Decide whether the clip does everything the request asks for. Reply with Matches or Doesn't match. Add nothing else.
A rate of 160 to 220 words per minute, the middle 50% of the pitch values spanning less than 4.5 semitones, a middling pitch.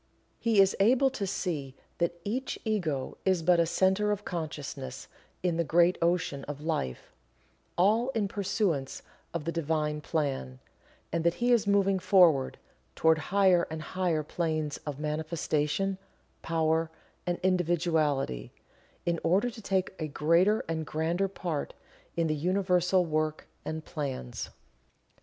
Doesn't match